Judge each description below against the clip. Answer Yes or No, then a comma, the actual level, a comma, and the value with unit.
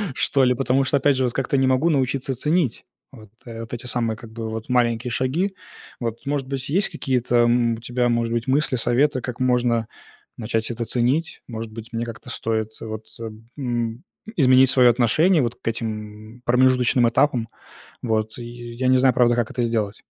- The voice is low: Yes, low, 120 Hz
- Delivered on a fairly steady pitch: Yes, narrow, 2.3 semitones